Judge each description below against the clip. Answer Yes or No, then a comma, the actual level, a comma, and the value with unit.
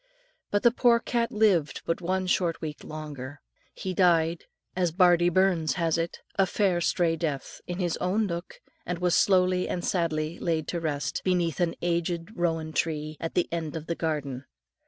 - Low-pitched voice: No, medium, 170 Hz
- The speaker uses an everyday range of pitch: No, narrow, 2.3 semitones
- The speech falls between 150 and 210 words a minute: Yes, average, 175 wpm